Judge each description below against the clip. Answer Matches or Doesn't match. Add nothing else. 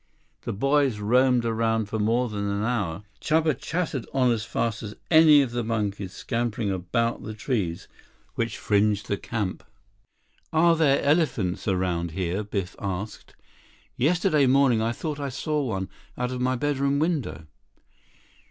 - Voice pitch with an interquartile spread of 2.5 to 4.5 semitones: Doesn't match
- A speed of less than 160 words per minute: Matches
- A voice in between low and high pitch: Doesn't match